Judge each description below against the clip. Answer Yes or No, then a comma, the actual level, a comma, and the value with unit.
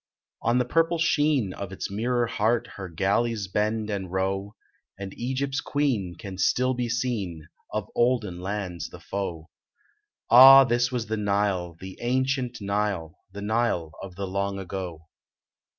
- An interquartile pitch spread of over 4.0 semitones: Yes, average, 4.4 semitones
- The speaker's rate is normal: Yes, average, 150 wpm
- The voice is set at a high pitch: No, low, 105 Hz